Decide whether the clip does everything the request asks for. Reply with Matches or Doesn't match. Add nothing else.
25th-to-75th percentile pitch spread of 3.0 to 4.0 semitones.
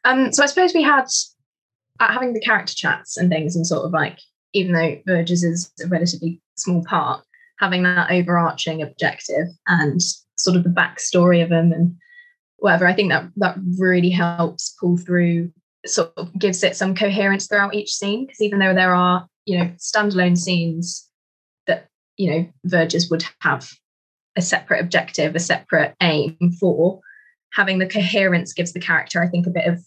Doesn't match